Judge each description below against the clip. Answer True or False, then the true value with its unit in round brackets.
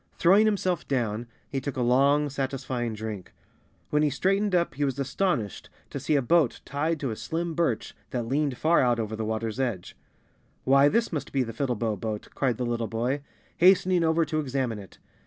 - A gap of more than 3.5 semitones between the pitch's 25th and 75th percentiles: True (5.2 semitones)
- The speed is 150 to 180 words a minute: False (195 wpm)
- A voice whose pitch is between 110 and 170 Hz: True (135 Hz)